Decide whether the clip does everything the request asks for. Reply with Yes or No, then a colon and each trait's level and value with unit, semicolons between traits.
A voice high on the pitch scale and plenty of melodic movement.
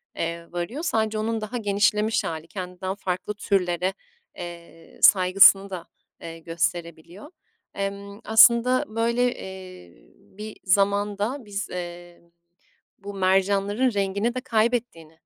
No: high, 195 Hz; average, 3.4 semitones